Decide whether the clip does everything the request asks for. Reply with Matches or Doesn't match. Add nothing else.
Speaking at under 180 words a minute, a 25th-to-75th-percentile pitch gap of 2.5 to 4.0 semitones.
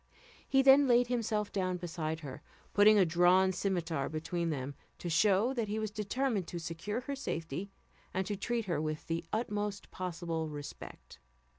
Doesn't match